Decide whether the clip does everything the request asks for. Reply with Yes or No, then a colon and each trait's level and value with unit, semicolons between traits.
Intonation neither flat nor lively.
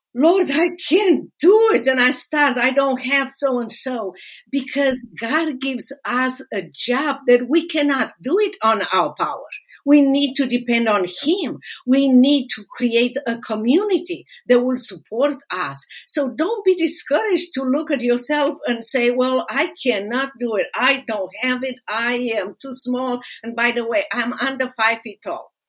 Yes: average, 3.2 semitones